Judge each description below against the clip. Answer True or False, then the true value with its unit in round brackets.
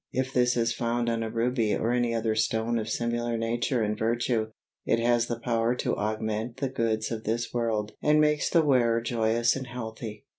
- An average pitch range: False (1.4 semitones)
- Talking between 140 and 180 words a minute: False (195 wpm)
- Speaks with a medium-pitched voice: False (115 Hz)